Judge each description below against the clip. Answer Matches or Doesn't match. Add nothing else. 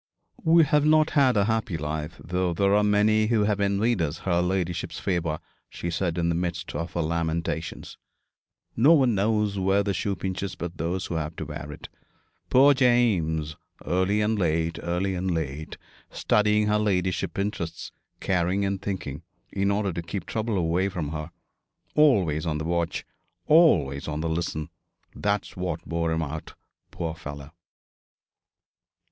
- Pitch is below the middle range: Matches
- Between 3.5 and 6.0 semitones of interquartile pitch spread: Matches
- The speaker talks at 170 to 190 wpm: Doesn't match